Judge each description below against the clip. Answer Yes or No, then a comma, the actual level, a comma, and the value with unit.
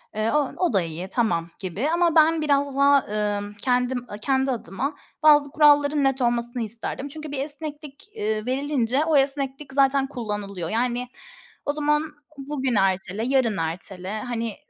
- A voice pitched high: Yes, very high, 260 Hz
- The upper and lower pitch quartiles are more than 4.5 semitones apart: Yes, average, 5.2 semitones